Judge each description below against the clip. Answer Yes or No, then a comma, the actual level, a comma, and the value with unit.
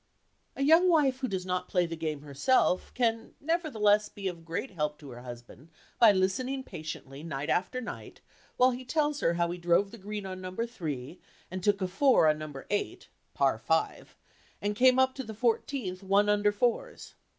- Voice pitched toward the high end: Yes, high, 200 Hz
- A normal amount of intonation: No, wide, 6.9 semitones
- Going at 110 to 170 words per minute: No, average, 190 wpm